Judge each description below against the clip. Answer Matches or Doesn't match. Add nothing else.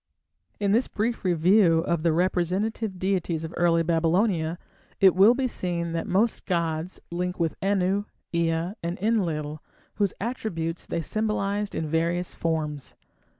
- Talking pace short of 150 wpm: Matches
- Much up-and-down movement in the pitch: Doesn't match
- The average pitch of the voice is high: Doesn't match